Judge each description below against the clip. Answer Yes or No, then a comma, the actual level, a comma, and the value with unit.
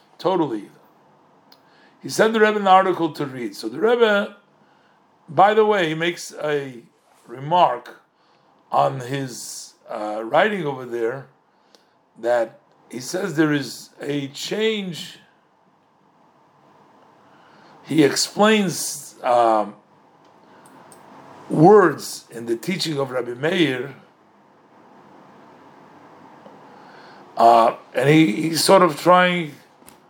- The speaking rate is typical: No, slow, 100 wpm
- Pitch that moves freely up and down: Yes, wide, 6.7 semitones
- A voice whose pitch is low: No, medium, 160 Hz